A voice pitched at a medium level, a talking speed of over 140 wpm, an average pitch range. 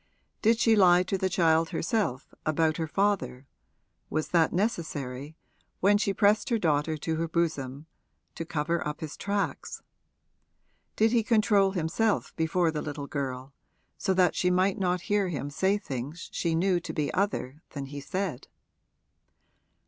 Yes: medium, 170 Hz; average, 155 wpm; average, 4.7 semitones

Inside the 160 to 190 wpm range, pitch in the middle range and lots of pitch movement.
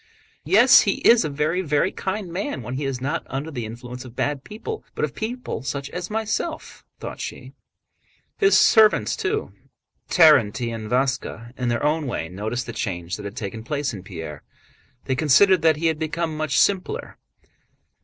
Yes: average, 170 wpm; medium, 145 Hz; wide, 7.2 semitones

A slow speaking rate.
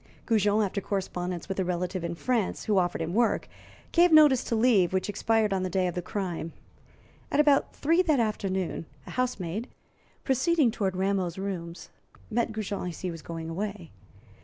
No: average, 175 wpm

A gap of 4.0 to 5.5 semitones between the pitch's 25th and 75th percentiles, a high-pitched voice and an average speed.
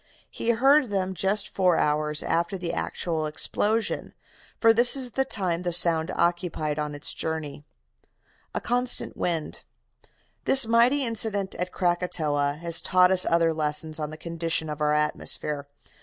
No: average, 4.9 semitones; medium, 170 Hz; average, 155 wpm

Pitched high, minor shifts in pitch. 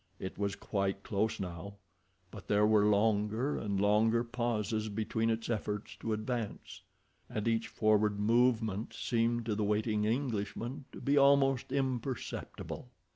No: low, 110 Hz; narrow, 2.3 semitones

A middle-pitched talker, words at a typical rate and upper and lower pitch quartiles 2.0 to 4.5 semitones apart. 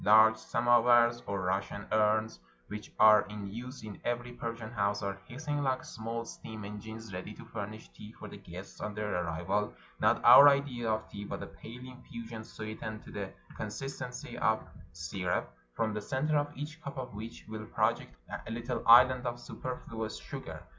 No: low, 110 Hz; average, 175 wpm; average, 2.7 semitones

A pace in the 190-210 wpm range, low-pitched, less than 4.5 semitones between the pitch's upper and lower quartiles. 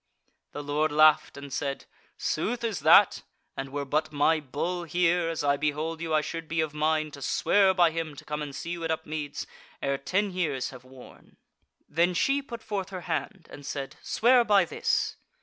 No: average, 195 wpm; medium, 155 Hz; average, 3.5 semitones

